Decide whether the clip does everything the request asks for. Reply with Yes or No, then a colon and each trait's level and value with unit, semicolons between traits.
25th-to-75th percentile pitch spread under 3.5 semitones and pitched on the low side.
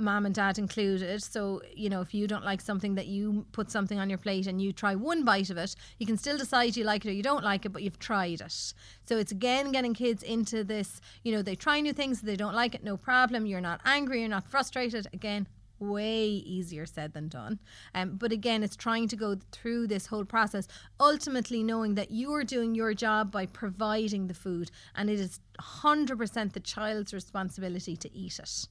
No: average, 2.9 semitones; high, 210 Hz